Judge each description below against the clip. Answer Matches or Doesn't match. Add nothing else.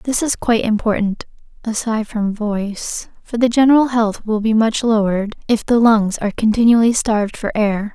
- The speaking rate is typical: Matches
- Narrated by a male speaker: Doesn't match